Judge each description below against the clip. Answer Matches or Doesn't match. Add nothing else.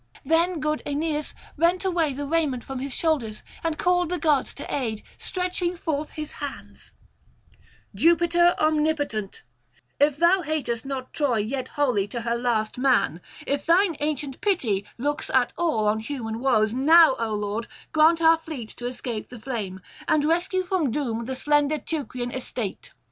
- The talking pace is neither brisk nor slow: Matches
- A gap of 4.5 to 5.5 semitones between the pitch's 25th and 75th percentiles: Matches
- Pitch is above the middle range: Matches